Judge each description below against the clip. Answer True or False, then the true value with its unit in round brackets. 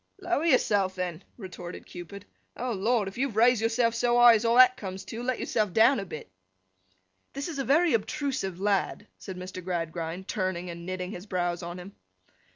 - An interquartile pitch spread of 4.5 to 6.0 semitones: True (5.0 semitones)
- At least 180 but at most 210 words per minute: True (185 wpm)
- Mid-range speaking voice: False (200 Hz)